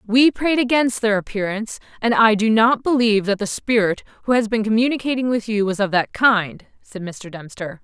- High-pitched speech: Yes, high, 220 Hz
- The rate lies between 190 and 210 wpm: Yes, average, 200 wpm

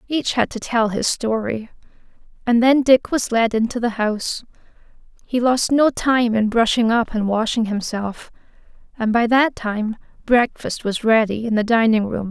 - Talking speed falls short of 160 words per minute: No, average, 170 wpm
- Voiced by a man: No, female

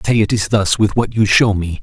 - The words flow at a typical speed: No, fast, 295 wpm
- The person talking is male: Yes, male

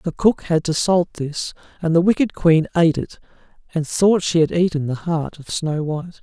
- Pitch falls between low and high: Yes, medium, 165 Hz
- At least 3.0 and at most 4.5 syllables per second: No, 5.1 syllables/s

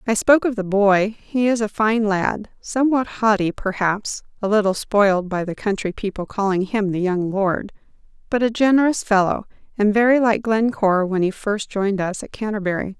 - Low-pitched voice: No, high, 210 Hz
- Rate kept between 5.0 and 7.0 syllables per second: Yes, 5.2 syllables/s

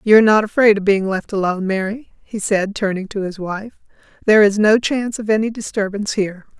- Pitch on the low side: No, high, 205 Hz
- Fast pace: Yes, fast, 210 wpm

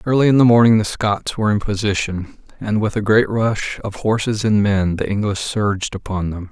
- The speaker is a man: Yes, male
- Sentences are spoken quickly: Yes, fast, 210 wpm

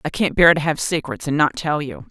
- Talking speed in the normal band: No, fast, 285 wpm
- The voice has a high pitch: No, medium, 155 Hz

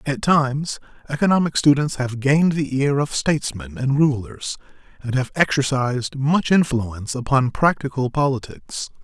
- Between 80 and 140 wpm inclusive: Yes, slow, 135 wpm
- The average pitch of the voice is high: No, medium, 140 Hz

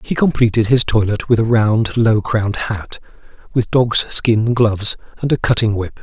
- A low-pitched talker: Yes, low, 110 Hz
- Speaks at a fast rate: No, average, 180 wpm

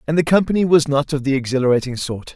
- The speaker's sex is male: Yes, male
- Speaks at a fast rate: Yes, fast, 230 wpm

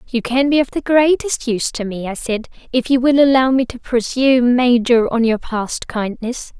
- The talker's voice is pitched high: Yes, high, 245 Hz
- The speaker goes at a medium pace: No, fast, 210 wpm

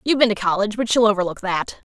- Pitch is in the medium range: No, high, 210 Hz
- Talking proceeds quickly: Yes, fast, 250 wpm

